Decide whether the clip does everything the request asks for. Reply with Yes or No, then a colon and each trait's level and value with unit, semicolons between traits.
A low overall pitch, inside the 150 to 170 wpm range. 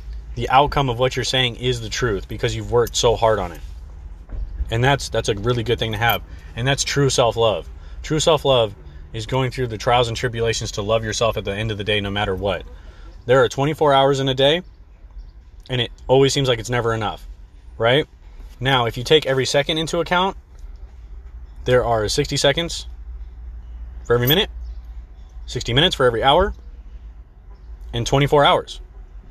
No: low, 110 Hz; average, 180 wpm